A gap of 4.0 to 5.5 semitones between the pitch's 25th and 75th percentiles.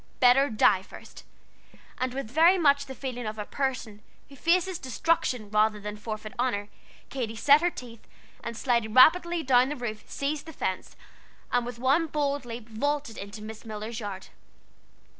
Yes: average, 4.7 semitones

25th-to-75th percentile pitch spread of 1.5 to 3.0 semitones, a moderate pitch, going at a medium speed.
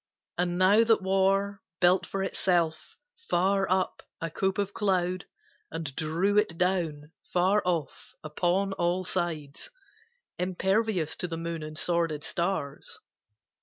No: narrow, 2.6 semitones; medium, 180 Hz; slow, 130 wpm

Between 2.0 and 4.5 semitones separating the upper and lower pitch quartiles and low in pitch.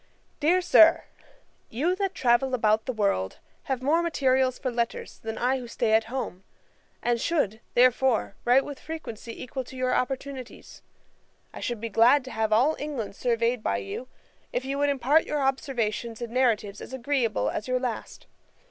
No: average, 3.1 semitones; very high, 250 Hz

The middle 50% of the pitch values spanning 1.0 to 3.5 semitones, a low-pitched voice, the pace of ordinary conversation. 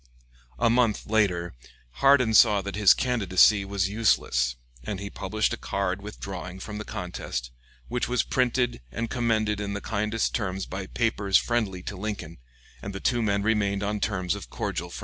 Yes: average, 2.7 semitones; low, 100 Hz; average, 170 wpm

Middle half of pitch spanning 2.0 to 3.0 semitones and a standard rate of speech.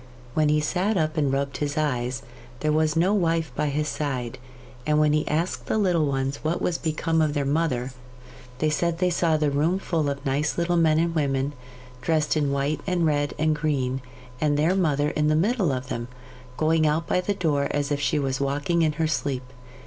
No: narrow, 2.6 semitones; fast, 210 wpm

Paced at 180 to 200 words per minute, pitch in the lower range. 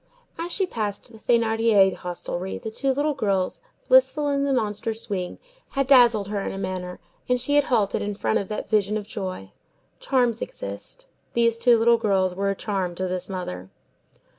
No: average, 185 wpm; high, 215 Hz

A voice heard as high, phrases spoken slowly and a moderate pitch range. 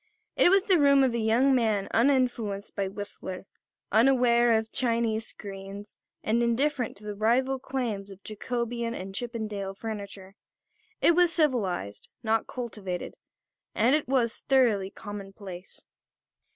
Yes: high, 225 Hz; slow, 130 wpm; average, 4.0 semitones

